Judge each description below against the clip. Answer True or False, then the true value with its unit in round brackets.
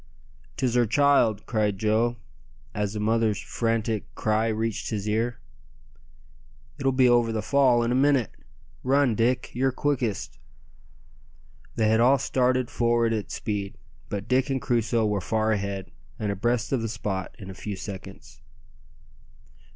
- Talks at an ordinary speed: True (145 wpm)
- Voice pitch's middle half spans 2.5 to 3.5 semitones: True (2.8 semitones)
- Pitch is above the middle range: False (115 Hz)